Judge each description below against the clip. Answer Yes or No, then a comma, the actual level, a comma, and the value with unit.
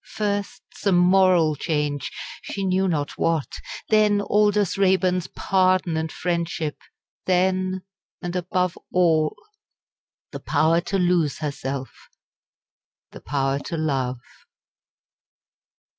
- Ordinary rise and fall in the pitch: Yes, average, 3.3 semitones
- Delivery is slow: Yes, slow, 100 wpm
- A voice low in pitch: No, medium, 180 Hz